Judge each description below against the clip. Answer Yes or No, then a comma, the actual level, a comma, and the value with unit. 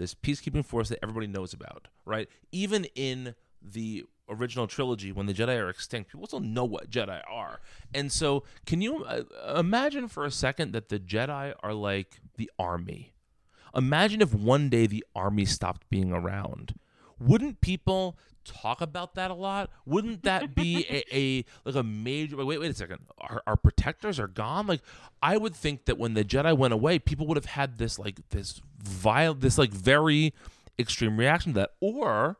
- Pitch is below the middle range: Yes, low, 130 Hz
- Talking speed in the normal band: Yes, average, 180 wpm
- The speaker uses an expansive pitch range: Yes, wide, 6.6 semitones